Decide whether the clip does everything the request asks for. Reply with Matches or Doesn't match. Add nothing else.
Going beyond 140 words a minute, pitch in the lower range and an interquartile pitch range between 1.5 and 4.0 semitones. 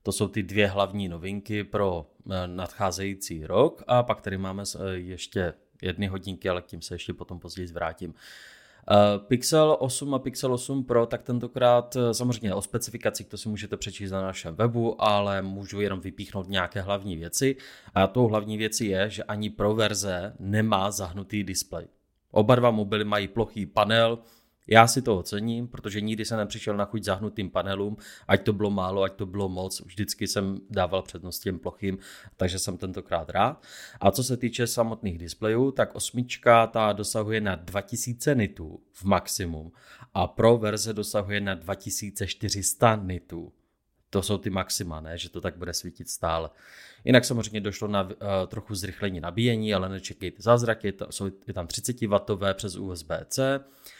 Matches